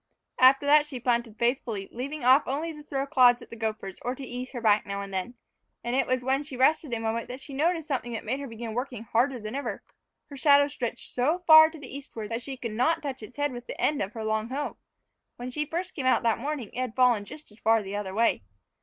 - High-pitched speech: Yes, very high, 250 Hz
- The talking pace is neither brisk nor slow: No, fast, 260 wpm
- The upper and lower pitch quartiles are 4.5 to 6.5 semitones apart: No, average, 3.8 semitones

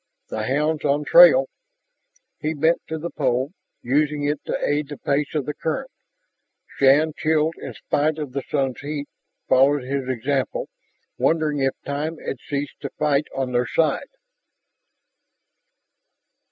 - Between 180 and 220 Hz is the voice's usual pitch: No, medium, 145 Hz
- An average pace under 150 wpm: Yes, average, 140 wpm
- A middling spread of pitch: No, narrow, 2.2 semitones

